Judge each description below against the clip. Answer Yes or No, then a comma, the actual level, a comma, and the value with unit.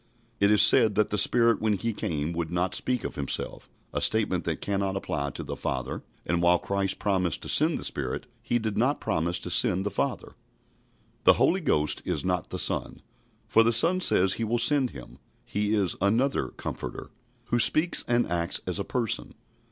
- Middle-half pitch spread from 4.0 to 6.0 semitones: Yes, average, 4.8 semitones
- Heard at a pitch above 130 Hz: No, low, 100 Hz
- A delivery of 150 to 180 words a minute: No, average, 195 wpm